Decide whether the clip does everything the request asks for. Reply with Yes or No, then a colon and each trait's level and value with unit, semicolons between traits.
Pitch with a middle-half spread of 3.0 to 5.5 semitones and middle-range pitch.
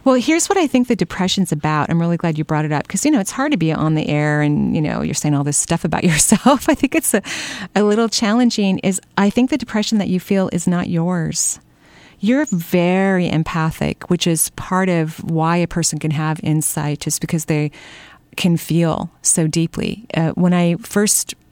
Yes: average, 4.8 semitones; medium, 180 Hz